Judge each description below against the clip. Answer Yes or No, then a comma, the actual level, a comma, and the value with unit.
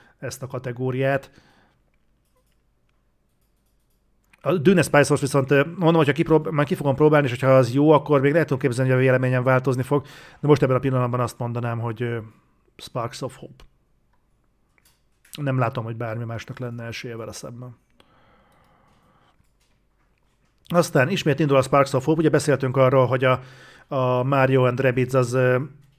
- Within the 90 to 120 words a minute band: No, average, 145 wpm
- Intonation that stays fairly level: Yes, narrow, 2.3 semitones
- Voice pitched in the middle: No, low, 130 Hz